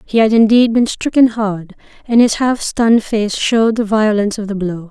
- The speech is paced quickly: Yes, fast, 210 wpm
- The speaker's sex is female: Yes, female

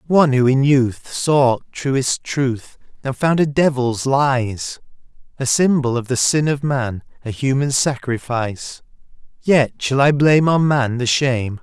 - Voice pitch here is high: No, low, 130 Hz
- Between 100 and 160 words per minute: Yes, average, 155 wpm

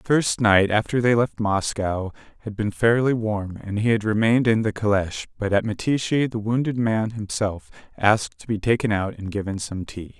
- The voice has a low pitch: Yes, low, 110 Hz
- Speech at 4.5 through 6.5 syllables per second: Yes, 5.1 syllables/s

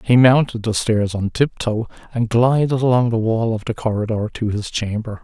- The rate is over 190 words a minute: Yes, fast, 205 wpm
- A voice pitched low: Yes, low, 115 Hz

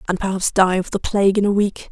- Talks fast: Yes, fast, 285 wpm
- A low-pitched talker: No, high, 195 Hz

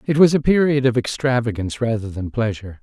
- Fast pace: No, average, 190 wpm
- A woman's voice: No, male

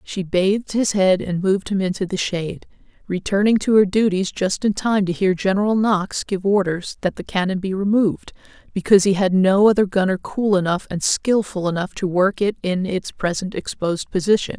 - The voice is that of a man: No, female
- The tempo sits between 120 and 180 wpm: No, average, 195 wpm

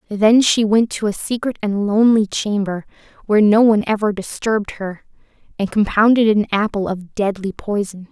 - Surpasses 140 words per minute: Yes, average, 165 wpm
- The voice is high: Yes, high, 210 Hz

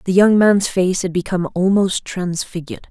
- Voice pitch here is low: No, medium, 185 Hz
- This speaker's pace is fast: No, average, 165 wpm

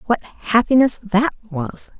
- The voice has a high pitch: Yes, high, 220 Hz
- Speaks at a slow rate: Yes, slow, 120 wpm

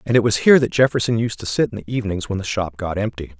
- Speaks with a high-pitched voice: No, low, 105 Hz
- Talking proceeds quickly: Yes, fast, 300 wpm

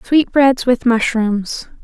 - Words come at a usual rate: No, slow, 100 wpm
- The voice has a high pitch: Yes, high, 245 Hz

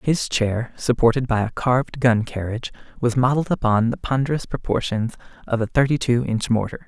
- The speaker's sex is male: Yes, male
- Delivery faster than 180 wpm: No, average, 165 wpm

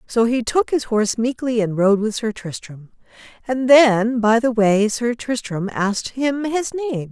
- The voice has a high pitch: Yes, high, 230 Hz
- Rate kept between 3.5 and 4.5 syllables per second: Yes, 4.3 syllables/s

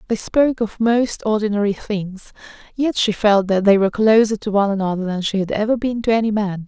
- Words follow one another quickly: Yes, fast, 215 wpm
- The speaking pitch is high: Yes, high, 210 Hz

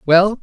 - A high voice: Yes, high, 195 Hz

